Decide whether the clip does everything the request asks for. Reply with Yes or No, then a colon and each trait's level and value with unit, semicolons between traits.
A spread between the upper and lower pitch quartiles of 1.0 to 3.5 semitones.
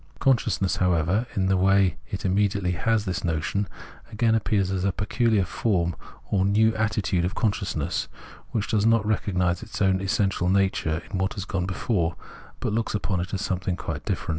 Yes: narrow, 2.6 semitones